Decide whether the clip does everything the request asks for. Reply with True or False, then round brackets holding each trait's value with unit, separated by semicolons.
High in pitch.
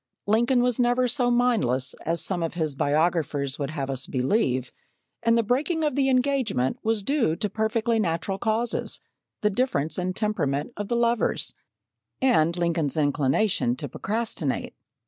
True (200 Hz)